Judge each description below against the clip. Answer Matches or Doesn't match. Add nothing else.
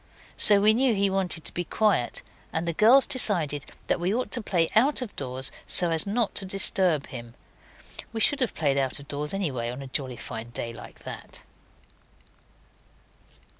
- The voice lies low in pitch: Doesn't match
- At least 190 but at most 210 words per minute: Doesn't match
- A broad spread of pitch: Matches